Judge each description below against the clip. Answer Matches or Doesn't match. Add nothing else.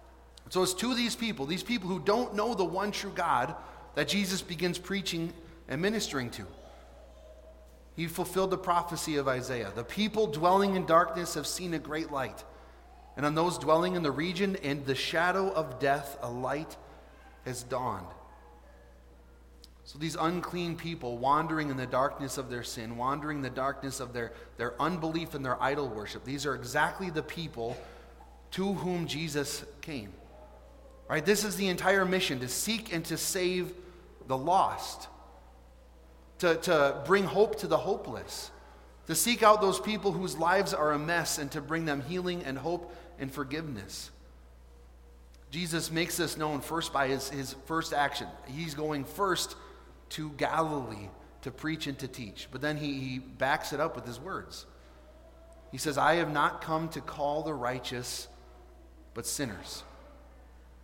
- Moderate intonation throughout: Doesn't match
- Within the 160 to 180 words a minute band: Matches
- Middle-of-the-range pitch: Matches